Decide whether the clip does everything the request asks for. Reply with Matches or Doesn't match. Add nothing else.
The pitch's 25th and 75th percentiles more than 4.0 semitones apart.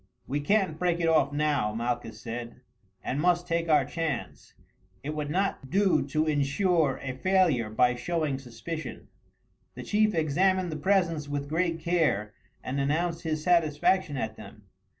Matches